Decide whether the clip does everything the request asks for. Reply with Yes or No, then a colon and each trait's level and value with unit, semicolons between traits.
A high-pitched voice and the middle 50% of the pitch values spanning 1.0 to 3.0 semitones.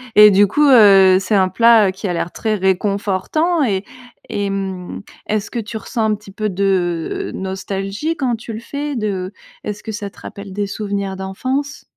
Yes: high, 205 Hz; average, 2.7 semitones